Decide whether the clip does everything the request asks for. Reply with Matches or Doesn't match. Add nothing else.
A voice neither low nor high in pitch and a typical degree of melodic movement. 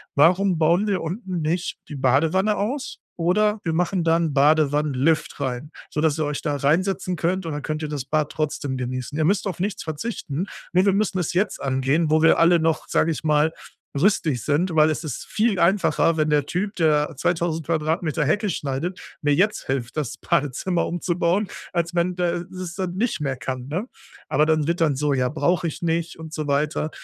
Matches